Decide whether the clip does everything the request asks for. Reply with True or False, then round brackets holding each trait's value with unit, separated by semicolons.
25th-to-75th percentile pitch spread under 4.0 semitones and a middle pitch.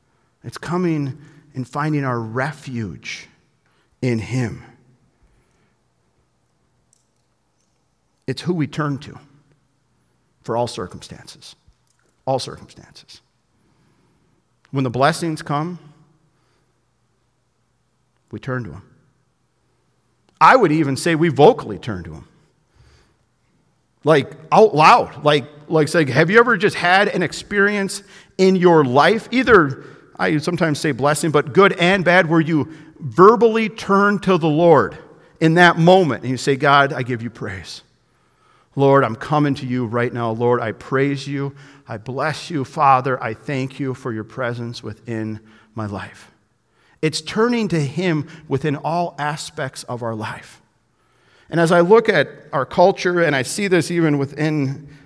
False (4.9 semitones; 145 Hz)